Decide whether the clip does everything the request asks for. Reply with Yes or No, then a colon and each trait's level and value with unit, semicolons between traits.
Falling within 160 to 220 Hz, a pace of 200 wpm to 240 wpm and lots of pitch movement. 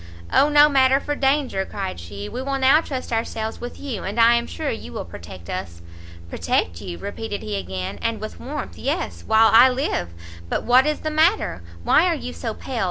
No: high, 235 Hz; fast, 205 wpm; wide, 6.9 semitones